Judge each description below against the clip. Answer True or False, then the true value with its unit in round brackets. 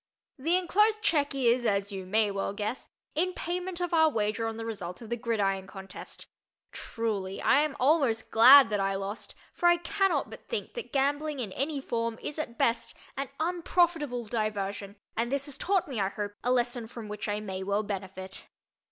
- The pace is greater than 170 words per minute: True (195 wpm)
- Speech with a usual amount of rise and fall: False (6.5 semitones)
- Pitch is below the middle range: False (235 Hz)